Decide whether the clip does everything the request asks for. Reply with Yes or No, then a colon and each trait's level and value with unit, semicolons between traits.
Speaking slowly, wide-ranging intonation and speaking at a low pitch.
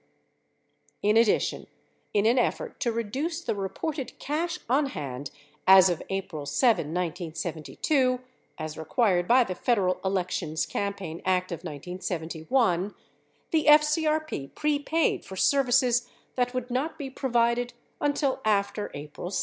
No: slow, 125 wpm; wide, 6.9 semitones; high, 215 Hz